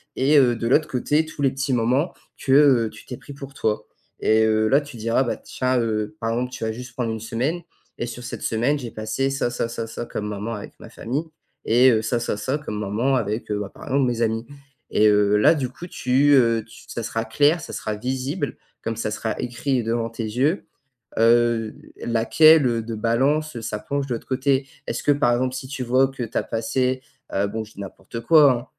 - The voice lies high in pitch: No, low, 120 Hz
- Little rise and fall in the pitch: No, average, 3.1 semitones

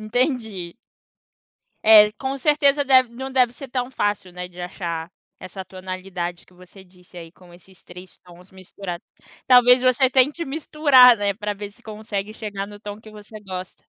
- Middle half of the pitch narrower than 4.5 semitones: No, average, 5.3 semitones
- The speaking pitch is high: Yes, high, 210 Hz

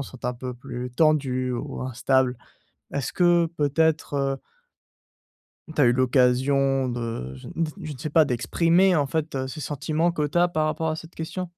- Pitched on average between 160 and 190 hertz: No, medium, 140 Hz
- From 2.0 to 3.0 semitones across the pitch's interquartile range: No, average, 4.0 semitones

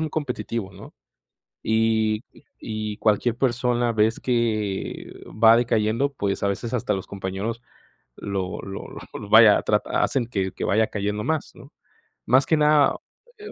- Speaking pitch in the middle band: No, low, 110 Hz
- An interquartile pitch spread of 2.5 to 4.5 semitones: Yes, average, 2.9 semitones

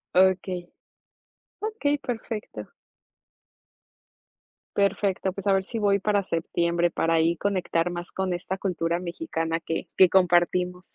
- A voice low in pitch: No, medium, 185 Hz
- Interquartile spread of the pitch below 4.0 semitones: Yes, narrow, 2.5 semitones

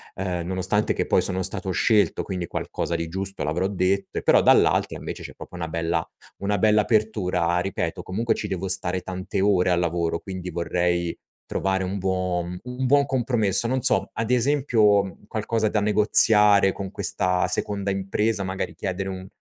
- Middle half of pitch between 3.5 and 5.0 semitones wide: No, average, 2.7 semitones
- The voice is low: Yes, very low, 95 Hz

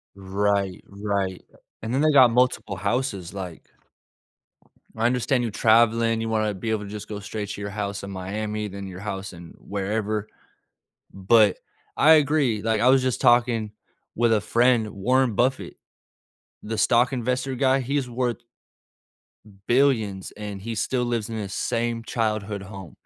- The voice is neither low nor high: No, low, 110 Hz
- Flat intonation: No, average, 3.3 semitones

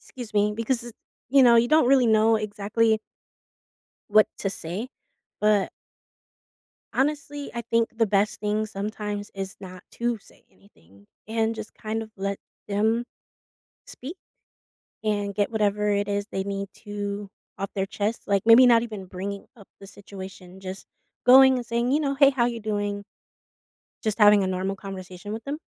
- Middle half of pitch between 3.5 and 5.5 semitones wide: No, narrow, 2.6 semitones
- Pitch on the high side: Yes, high, 210 Hz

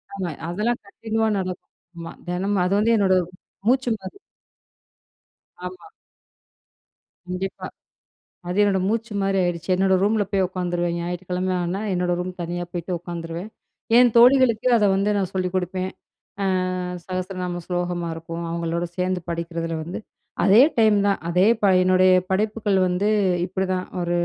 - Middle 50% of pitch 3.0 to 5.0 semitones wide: No, narrow, 2.4 semitones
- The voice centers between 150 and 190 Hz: Yes, medium, 185 Hz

